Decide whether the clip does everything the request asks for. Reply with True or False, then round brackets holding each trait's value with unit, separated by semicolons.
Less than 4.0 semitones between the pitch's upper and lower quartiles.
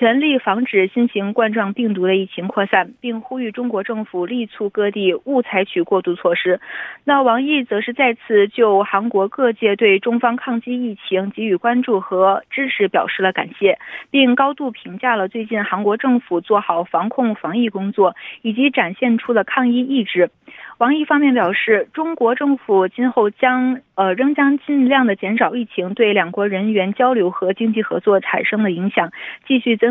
False (4.4 semitones)